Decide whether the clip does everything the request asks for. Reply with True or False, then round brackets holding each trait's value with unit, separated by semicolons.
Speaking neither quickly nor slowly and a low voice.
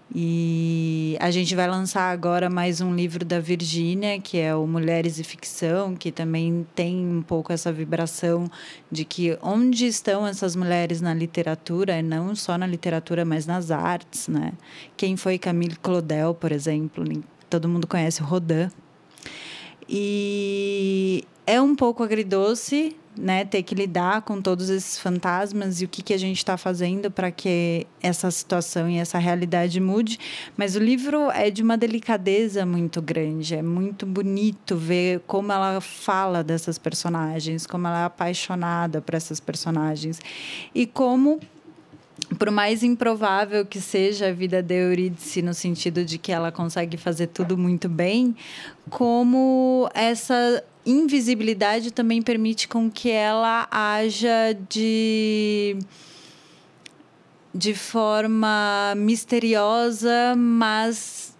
False (135 wpm; 185 Hz)